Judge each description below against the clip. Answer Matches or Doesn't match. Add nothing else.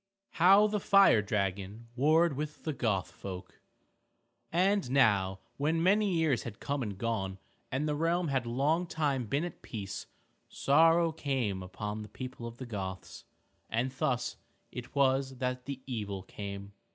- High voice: Doesn't match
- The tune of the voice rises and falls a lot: Matches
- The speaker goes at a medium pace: Matches